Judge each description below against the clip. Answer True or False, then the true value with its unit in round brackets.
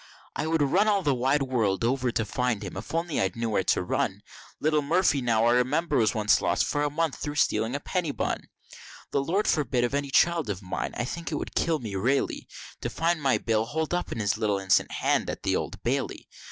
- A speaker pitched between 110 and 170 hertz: True (135 Hz)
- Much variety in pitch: True (5.8 semitones)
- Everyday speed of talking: False (230 wpm)